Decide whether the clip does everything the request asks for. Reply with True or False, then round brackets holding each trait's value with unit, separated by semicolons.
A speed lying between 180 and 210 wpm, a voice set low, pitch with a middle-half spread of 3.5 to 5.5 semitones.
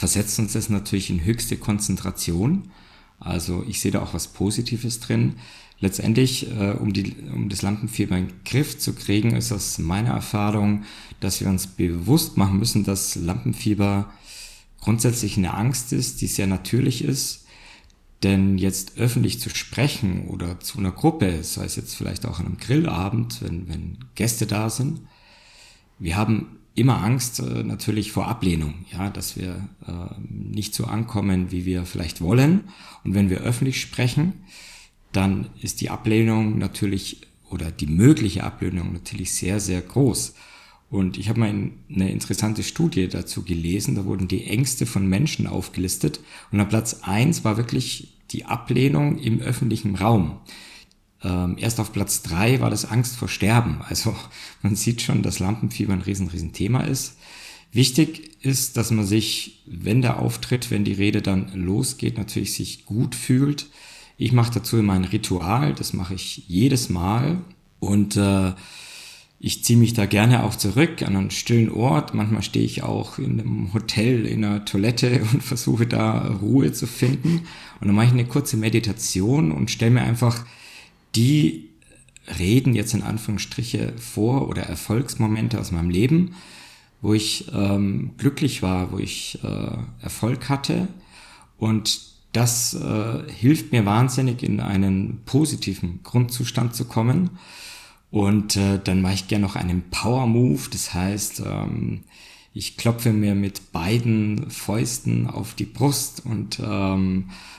False (155 wpm; 105 Hz; 4.2 semitones)